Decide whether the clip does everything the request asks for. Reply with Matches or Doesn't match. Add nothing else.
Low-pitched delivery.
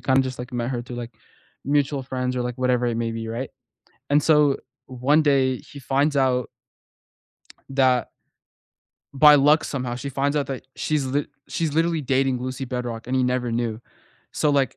Matches